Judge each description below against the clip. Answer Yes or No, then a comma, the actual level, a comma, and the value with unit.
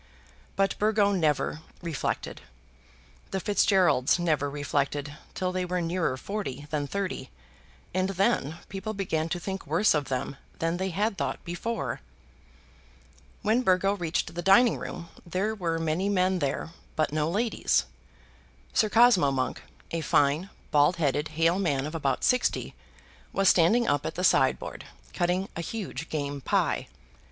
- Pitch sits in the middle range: Yes, medium, 175 Hz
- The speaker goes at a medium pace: Yes, average, 145 wpm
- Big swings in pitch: No, average, 4.6 semitones